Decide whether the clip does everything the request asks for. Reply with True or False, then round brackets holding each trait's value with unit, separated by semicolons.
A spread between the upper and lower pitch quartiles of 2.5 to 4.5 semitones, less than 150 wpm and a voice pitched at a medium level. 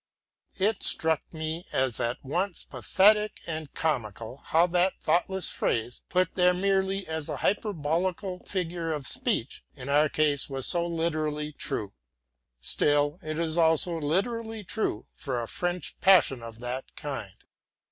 True (4.2 semitones; 140 wpm; 160 Hz)